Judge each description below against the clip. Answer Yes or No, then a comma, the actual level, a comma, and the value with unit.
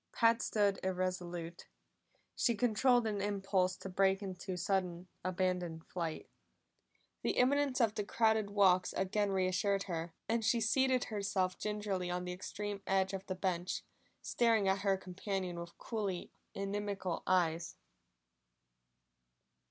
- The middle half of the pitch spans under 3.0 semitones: Yes, narrow, 2.4 semitones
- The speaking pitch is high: Yes, high, 195 Hz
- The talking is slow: Yes, slow, 130 wpm